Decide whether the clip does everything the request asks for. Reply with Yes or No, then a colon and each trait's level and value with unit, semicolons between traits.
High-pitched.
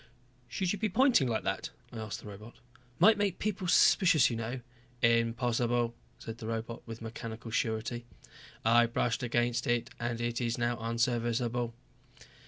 No: low, 120 Hz